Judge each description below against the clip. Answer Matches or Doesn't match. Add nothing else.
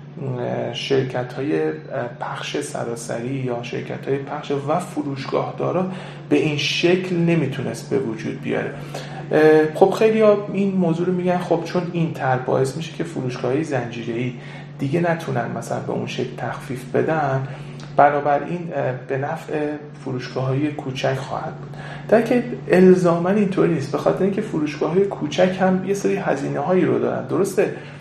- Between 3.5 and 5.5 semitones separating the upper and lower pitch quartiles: Matches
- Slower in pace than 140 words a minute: Doesn't match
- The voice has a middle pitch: Matches